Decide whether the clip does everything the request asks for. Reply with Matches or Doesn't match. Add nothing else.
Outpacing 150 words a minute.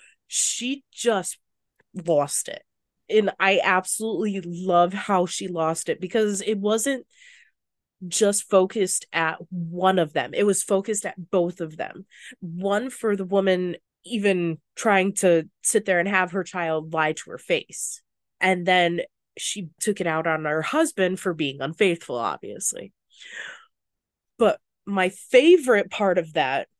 Doesn't match